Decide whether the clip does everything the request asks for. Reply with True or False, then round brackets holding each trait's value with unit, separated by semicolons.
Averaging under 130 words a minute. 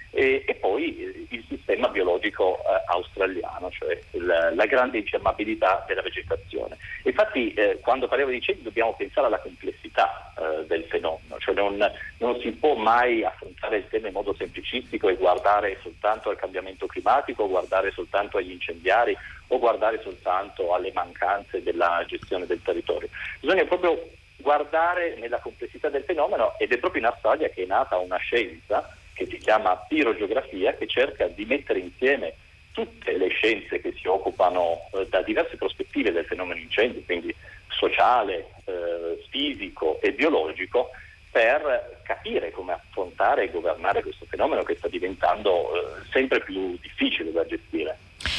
False (150 wpm)